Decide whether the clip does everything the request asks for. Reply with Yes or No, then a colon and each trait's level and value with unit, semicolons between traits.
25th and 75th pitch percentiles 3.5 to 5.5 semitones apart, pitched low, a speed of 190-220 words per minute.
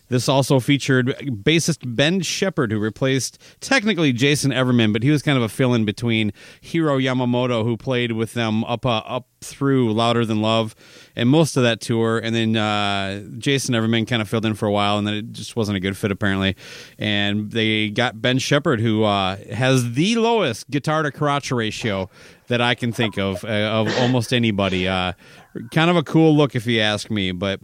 Yes: average, 4.1 semitones; low, 120 Hz; average, 200 wpm